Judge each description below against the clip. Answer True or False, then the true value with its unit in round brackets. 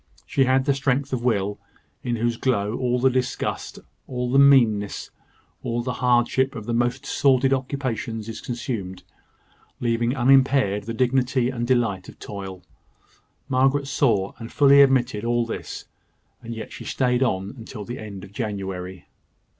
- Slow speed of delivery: False (155 wpm)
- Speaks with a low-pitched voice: True (120 Hz)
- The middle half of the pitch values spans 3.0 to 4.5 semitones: True (3.3 semitones)